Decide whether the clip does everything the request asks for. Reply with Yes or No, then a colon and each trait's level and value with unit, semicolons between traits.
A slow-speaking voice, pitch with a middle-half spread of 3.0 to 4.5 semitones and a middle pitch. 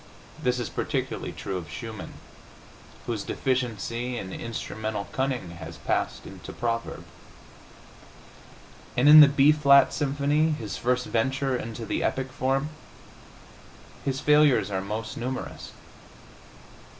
No: slow, 115 wpm; average, 3.8 semitones; low, 125 Hz